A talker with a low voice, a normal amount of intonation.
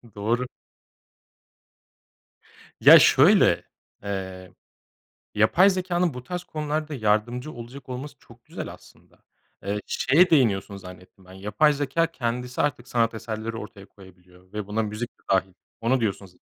No: low, 115 Hz; wide, 5.8 semitones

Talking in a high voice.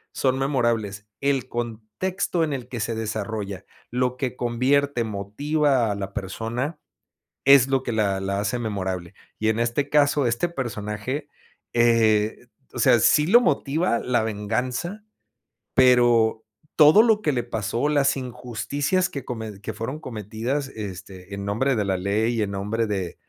No: low, 120 Hz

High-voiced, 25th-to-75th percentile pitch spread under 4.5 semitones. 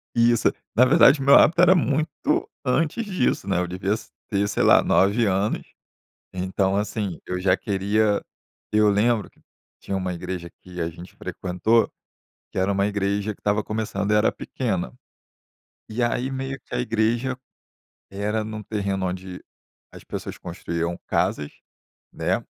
No: low, 105 Hz; average, 3.8 semitones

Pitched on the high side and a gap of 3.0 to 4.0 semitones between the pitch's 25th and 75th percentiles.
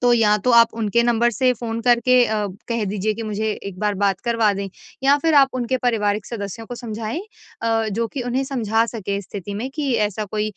No: high, 225 Hz; narrow, 2.6 semitones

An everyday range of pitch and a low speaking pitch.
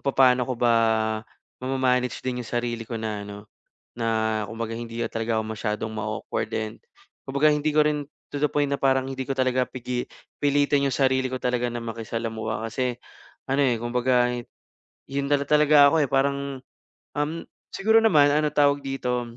Yes: average, 3.4 semitones; low, 130 Hz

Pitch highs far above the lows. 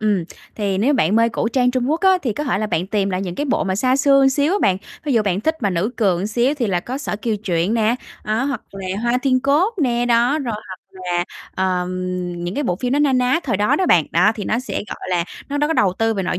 Yes: wide, 5.8 semitones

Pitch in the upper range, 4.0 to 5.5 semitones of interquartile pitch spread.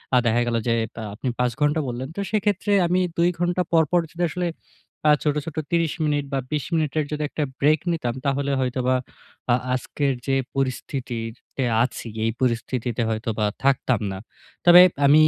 No: medium, 140 Hz; average, 4.5 semitones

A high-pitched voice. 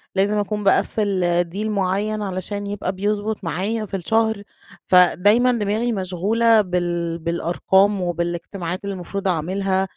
Yes: high, 195 Hz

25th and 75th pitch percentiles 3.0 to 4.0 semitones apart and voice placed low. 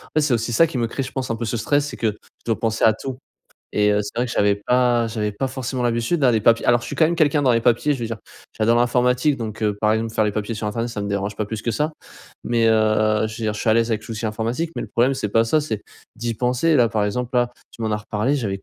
No: narrow, 2.5 semitones; low, 115 Hz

